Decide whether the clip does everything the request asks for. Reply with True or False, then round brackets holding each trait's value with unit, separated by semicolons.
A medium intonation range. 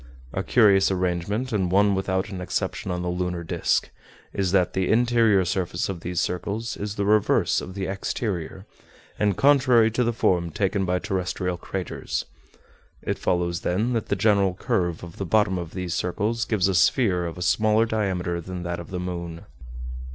True (3.0 semitones)